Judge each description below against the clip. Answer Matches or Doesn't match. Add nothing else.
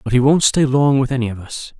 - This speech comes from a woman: Doesn't match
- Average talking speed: Doesn't match